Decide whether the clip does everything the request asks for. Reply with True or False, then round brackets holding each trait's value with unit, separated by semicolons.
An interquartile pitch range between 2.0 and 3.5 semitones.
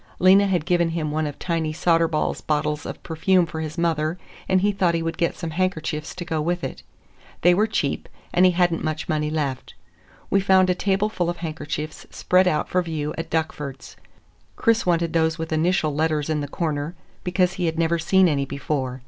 True (2.7 semitones)